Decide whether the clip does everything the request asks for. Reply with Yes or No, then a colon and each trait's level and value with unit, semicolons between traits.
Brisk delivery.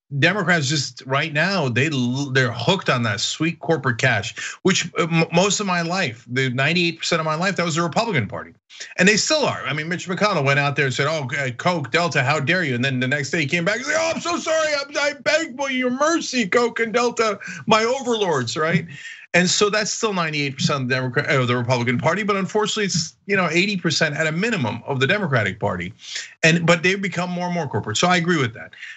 Yes: fast, 230 wpm